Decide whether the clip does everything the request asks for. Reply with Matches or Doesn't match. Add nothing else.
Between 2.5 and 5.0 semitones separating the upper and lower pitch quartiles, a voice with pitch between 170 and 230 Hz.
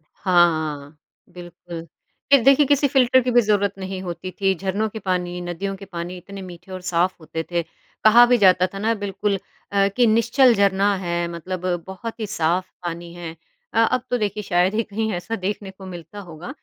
Matches